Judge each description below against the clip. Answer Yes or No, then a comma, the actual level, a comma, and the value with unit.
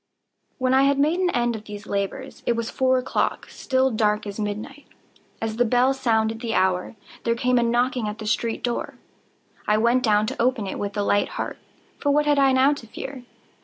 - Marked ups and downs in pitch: No, average, 3.4 semitones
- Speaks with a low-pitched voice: No, high, 240 Hz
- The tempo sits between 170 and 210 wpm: Yes, average, 200 wpm